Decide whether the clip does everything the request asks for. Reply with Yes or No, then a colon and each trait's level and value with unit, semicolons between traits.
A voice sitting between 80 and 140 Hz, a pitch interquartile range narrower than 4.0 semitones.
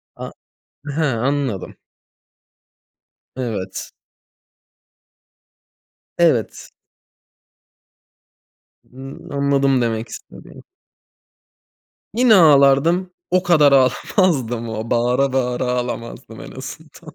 Yes: low, 135 Hz; average, 3.4 semitones